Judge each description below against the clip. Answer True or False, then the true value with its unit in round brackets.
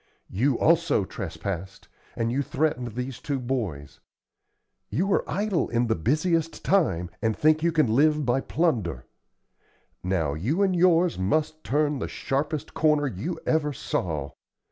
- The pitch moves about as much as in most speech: False (6.5 semitones)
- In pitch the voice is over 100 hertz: True (140 Hz)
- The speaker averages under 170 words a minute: True (145 wpm)